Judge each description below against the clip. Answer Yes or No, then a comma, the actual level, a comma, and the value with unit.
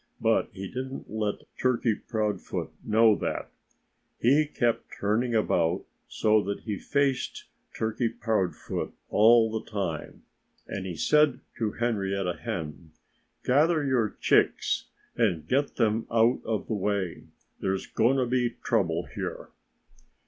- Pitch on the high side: No, low, 110 Hz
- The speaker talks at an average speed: No, slow, 125 wpm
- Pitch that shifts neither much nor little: Yes, average, 3.7 semitones